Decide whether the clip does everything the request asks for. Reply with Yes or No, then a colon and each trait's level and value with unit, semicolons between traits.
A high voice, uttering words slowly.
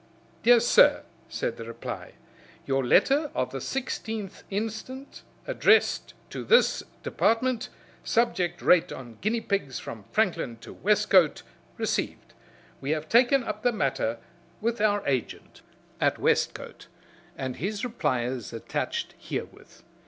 Yes: high, 205 Hz; slow, 125 wpm